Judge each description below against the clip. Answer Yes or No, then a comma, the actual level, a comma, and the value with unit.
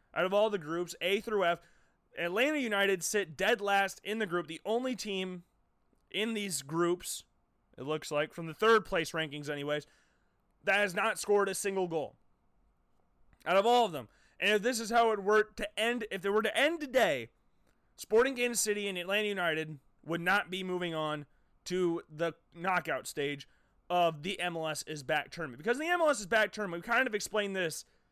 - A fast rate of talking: No, average, 190 wpm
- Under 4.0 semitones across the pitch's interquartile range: No, average, 4.6 semitones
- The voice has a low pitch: No, high, 190 Hz